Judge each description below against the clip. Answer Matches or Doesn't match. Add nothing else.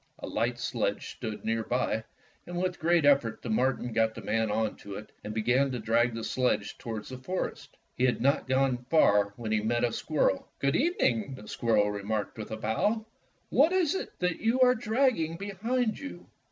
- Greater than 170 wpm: Matches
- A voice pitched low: Matches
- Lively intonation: Matches